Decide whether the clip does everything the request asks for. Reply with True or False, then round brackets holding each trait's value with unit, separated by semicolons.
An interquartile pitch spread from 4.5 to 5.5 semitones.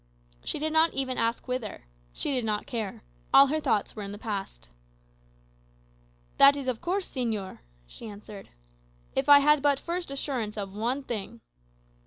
True (5.2 semitones)